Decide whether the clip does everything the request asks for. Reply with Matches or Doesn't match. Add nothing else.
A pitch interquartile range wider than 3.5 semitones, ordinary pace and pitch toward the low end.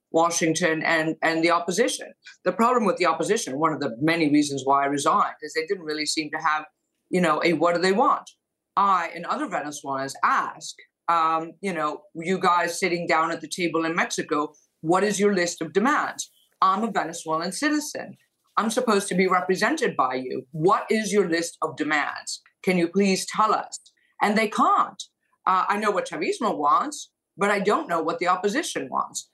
Doesn't match